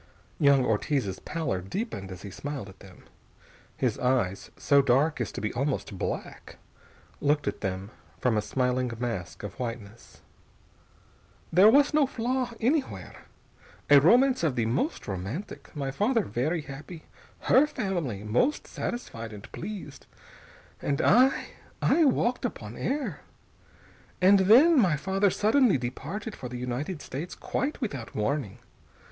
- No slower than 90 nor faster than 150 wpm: Yes, average, 140 wpm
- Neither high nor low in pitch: Yes, medium, 145 Hz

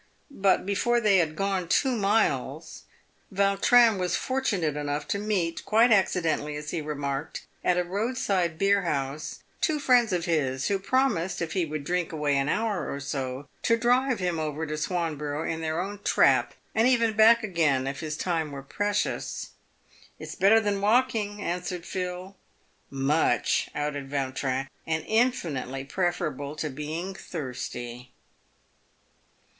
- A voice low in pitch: No, medium, 175 Hz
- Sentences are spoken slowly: No, average, 155 wpm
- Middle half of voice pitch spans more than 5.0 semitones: Yes, wide, 5.6 semitones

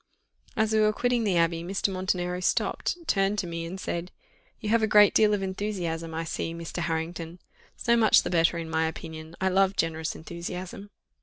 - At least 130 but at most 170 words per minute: No, average, 190 wpm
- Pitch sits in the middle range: Yes, medium, 180 Hz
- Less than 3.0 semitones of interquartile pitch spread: No, average, 3.7 semitones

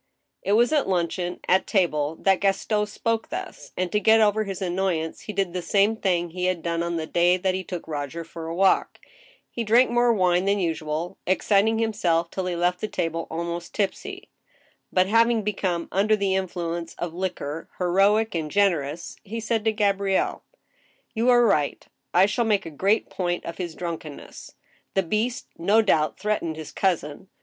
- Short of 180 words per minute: No, average, 185 wpm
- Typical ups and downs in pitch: Yes, average, 3.8 semitones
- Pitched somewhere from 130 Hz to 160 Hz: No, medium, 185 Hz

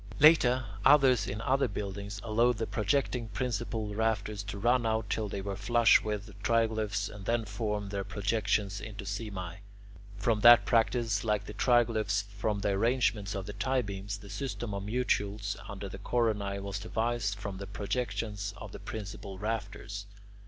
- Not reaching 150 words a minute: No, average, 165 wpm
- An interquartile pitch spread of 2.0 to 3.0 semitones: Yes, narrow, 2.4 semitones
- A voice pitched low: Yes, low, 105 Hz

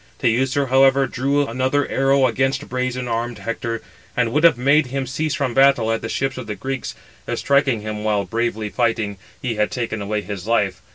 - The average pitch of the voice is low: Yes, low, 125 Hz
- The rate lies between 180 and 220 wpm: Yes, average, 190 wpm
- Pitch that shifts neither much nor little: Yes, average, 3.1 semitones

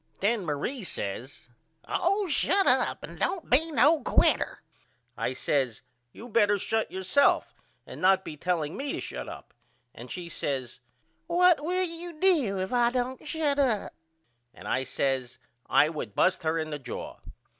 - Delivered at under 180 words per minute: Yes, average, 165 wpm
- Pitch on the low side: No, high, 205 Hz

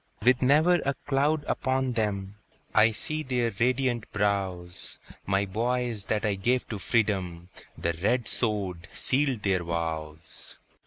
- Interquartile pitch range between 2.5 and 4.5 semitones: No, average, 5.0 semitones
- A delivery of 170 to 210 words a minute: No, slow, 135 wpm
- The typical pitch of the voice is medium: No, low, 110 Hz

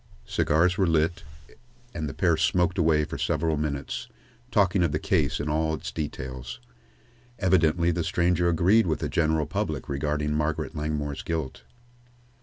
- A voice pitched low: Yes, very low, 80 Hz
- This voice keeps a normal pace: Yes, average, 155 wpm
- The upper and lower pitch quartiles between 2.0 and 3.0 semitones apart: Yes, narrow, 2.5 semitones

